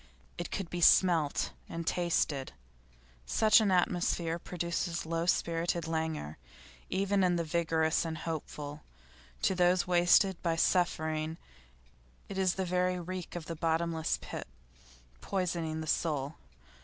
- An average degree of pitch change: No, narrow, 2.0 semitones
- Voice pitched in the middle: Yes, medium, 170 Hz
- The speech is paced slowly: Yes, slow, 130 wpm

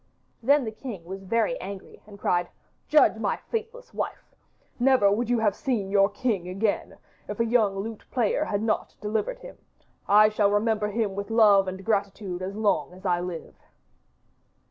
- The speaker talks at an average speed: Yes, average, 170 wpm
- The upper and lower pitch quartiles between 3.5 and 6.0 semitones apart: No, average, 2.9 semitones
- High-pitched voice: Yes, high, 210 Hz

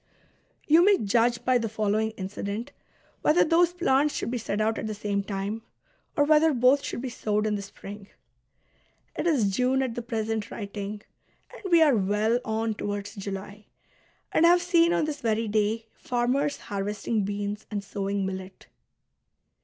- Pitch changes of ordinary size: Yes, average, 4.5 semitones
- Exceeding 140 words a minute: Yes, average, 170 wpm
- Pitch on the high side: Yes, high, 220 Hz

